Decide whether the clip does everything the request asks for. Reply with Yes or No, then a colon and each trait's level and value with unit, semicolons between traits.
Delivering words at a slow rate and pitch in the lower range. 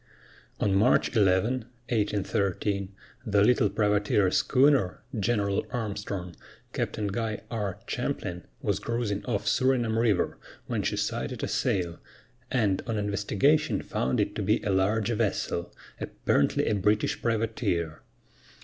Yes: slow, 120 wpm; low, 105 Hz